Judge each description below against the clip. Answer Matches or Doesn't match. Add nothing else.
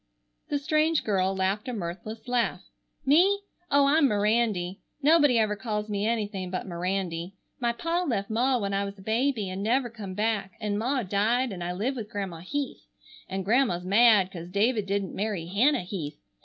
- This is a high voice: Matches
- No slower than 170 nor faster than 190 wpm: Matches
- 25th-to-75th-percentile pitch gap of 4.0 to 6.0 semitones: Matches